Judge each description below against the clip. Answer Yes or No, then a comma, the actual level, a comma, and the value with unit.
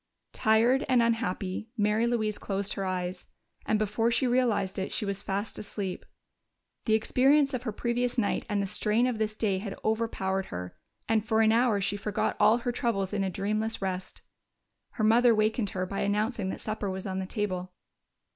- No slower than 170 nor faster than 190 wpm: Yes, average, 185 wpm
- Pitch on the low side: No, high, 215 Hz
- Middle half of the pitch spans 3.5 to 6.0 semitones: No, average, 3.0 semitones